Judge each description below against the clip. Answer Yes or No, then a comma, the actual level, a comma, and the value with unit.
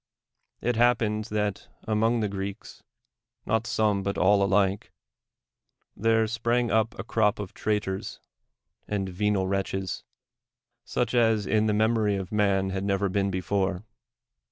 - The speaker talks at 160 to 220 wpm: No, slow, 135 wpm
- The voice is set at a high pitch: No, low, 105 Hz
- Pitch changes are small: Yes, narrow, 2.2 semitones